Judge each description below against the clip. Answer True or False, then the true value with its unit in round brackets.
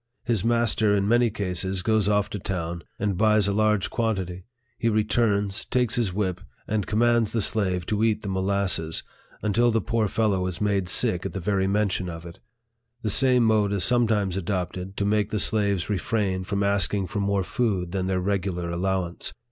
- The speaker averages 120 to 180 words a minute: False (190 wpm)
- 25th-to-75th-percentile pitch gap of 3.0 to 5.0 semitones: False (2.6 semitones)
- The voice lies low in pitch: True (100 Hz)